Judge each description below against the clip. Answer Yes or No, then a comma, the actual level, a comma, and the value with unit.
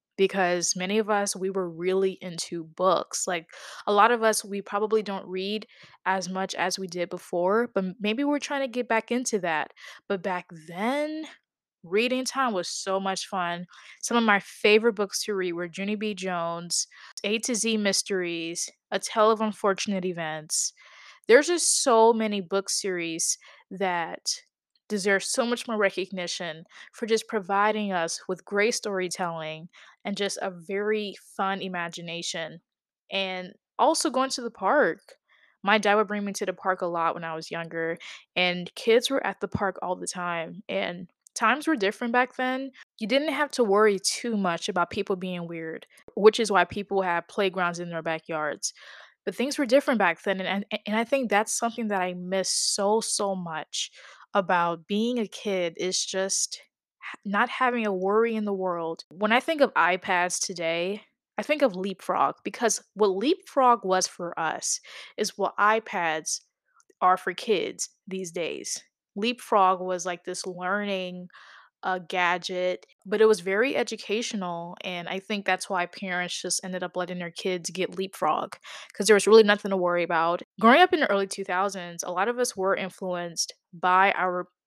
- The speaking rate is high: No, average, 175 wpm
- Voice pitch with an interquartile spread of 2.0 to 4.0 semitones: Yes, average, 3.4 semitones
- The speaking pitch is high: Yes, high, 195 Hz